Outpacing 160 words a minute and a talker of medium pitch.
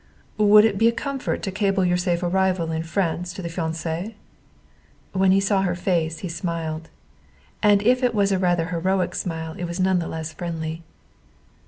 Yes: average, 185 wpm; medium, 180 Hz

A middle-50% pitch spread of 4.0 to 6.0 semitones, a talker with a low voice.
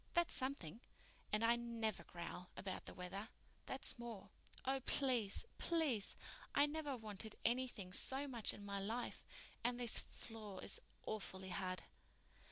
No: average, 4.5 semitones; high, 225 Hz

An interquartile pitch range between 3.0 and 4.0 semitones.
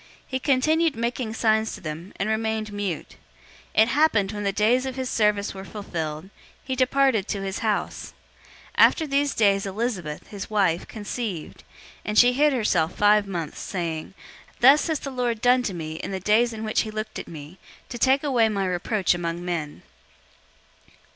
No: average, 4.5 semitones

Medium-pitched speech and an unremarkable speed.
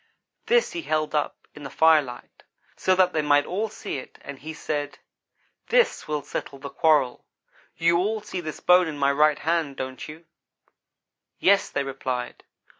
Yes: medium, 155 Hz; average, 170 wpm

